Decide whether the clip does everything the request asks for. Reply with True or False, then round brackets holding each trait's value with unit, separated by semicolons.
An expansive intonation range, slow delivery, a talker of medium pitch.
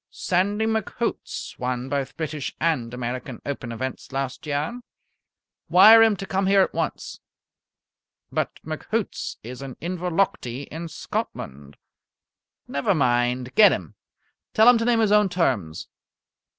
True (7.7 semitones; 130 wpm; 155 Hz)